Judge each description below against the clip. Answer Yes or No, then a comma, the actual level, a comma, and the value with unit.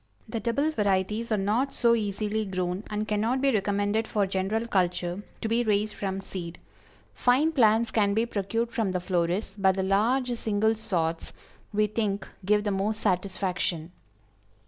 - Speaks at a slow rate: No, average, 160 wpm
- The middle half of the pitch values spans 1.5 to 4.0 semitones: Yes, average, 2.8 semitones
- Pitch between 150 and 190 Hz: No, high, 210 Hz